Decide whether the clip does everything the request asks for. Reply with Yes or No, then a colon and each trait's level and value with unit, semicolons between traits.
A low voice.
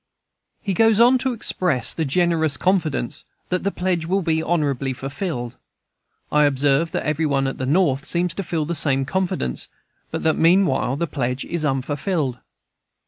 No: medium, 160 Hz